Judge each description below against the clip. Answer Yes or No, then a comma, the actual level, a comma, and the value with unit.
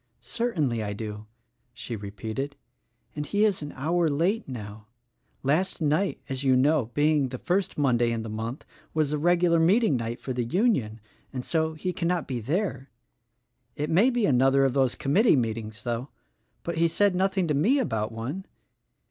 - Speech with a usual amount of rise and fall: No, wide, 6.7 semitones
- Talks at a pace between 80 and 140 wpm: No, average, 175 wpm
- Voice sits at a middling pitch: Yes, medium, 145 Hz